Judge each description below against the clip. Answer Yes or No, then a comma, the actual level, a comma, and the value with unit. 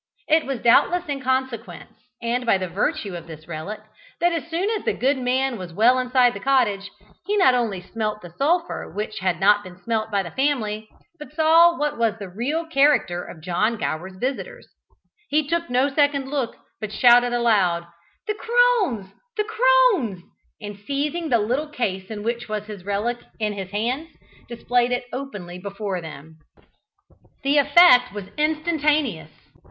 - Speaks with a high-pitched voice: Yes, high, 240 Hz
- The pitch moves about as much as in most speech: No, wide, 6.3 semitones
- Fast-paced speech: No, average, 165 wpm